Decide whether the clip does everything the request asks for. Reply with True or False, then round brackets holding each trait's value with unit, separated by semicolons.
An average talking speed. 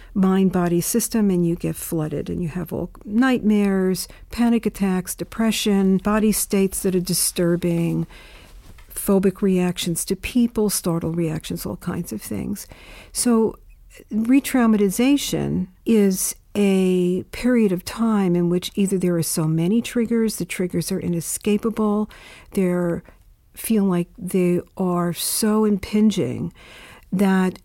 False (125 wpm)